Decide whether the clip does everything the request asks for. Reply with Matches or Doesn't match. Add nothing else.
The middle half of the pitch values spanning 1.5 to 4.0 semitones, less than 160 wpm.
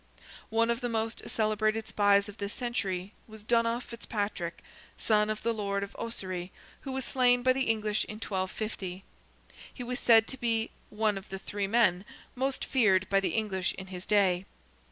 Doesn't match